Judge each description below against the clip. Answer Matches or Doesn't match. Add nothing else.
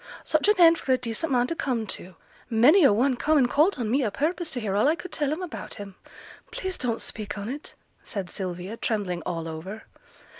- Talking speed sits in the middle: Doesn't match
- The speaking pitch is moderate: Doesn't match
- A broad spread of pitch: Matches